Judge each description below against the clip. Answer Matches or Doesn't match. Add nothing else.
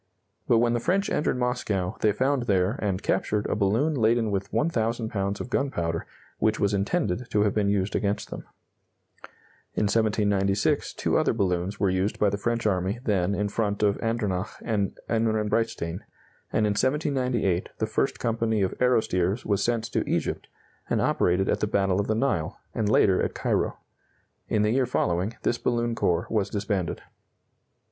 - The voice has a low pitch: Matches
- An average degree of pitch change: Matches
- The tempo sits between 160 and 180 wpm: Matches